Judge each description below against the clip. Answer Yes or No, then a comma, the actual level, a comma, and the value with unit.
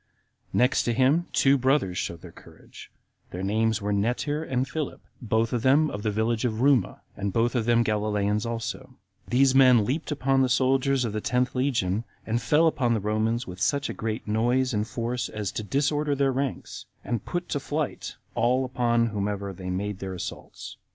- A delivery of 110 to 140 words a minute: No, average, 185 wpm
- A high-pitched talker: No, low, 120 Hz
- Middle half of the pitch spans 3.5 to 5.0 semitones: Yes, average, 3.9 semitones